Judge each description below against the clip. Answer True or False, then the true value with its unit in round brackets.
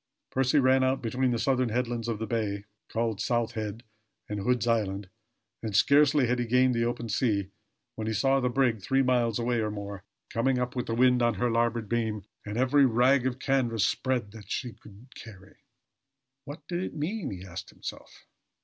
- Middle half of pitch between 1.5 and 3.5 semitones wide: True (2.9 semitones)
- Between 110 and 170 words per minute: False (195 wpm)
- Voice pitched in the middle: False (120 Hz)